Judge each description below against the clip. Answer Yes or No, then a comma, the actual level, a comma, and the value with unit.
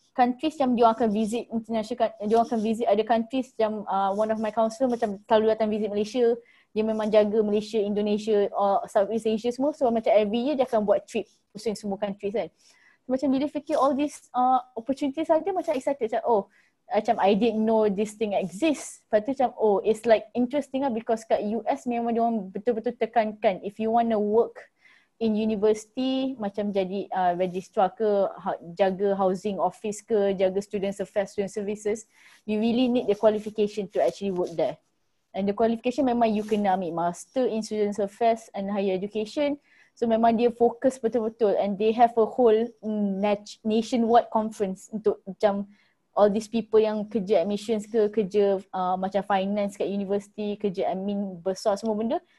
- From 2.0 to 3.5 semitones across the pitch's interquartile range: Yes, narrow, 2.5 semitones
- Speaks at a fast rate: Yes, fast, 180 wpm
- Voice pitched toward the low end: No, high, 220 Hz